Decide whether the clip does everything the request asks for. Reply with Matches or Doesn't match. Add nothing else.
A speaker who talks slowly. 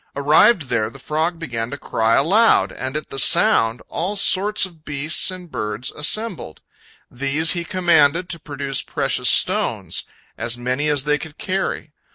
Doesn't match